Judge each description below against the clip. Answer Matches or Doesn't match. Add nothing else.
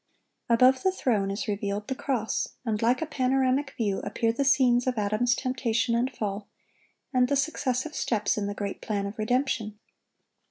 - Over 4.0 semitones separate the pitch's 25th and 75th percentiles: Doesn't match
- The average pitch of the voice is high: Matches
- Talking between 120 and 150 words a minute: Doesn't match